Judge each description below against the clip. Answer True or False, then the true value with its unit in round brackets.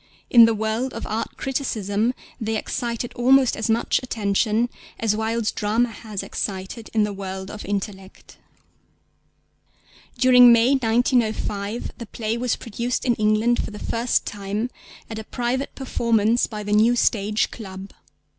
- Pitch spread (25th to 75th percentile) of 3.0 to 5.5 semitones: False (2.4 semitones)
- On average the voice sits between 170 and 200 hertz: False (225 Hz)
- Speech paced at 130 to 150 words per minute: True (145 wpm)